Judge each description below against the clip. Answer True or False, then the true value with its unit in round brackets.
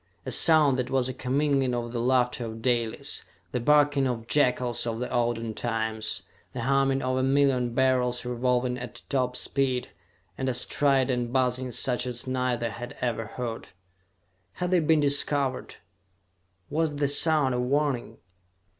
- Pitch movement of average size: False (2.1 semitones)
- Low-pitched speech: True (125 Hz)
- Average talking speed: True (155 wpm)